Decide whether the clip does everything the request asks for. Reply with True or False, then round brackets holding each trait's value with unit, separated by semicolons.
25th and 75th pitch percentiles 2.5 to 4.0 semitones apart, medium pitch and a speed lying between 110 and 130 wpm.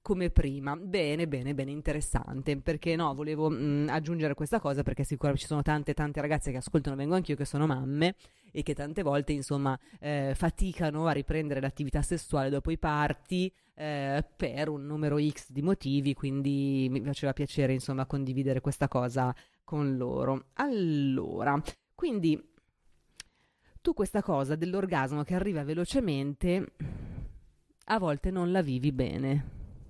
False (2.8 semitones; 150 Hz; 145 wpm)